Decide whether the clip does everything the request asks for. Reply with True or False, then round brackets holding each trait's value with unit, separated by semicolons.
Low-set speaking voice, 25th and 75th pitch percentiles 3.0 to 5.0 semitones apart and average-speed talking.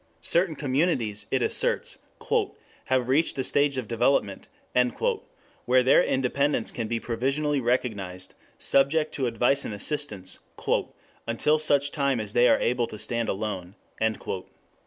False (125 Hz; 4.0 semitones; 130 wpm)